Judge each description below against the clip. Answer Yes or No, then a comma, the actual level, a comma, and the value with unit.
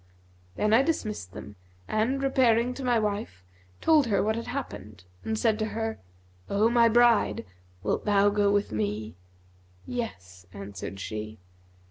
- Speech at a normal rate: Yes, average, 145 wpm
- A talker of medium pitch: No, high, 215 Hz